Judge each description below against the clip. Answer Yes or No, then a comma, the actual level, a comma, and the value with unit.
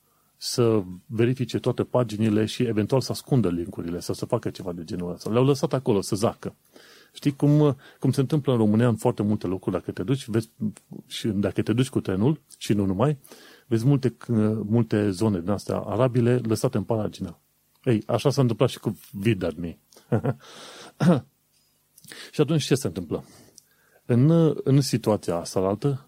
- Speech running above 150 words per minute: Yes, average, 165 wpm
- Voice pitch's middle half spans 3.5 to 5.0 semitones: Yes, average, 4.4 semitones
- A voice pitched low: Yes, low, 115 Hz